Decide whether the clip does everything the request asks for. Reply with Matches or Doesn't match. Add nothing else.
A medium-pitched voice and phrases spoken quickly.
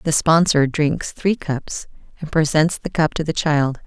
Doesn't match